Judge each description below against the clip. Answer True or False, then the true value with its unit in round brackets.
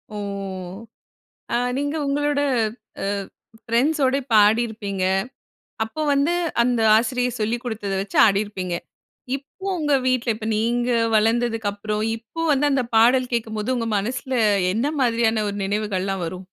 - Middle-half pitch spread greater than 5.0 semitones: False (3.4 semitones)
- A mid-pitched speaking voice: False (230 Hz)